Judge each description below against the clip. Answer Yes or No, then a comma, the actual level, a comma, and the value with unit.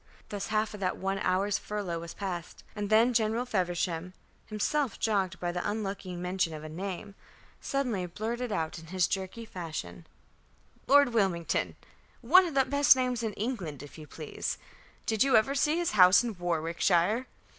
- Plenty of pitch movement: No, average, 4.8 semitones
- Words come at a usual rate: Yes, average, 165 wpm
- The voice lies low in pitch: No, high, 200 Hz